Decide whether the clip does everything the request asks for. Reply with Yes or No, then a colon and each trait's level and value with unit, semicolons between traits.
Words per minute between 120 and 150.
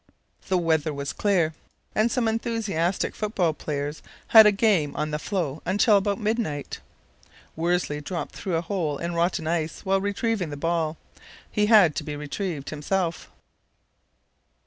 Yes: average, 145 wpm